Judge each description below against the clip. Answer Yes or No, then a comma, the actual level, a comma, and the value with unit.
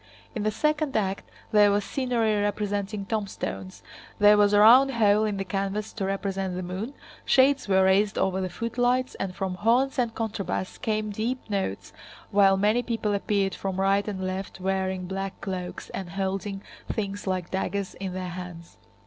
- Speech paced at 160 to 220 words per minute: Yes, average, 170 wpm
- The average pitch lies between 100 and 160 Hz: No, high, 200 Hz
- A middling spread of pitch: No, narrow, 2.2 semitones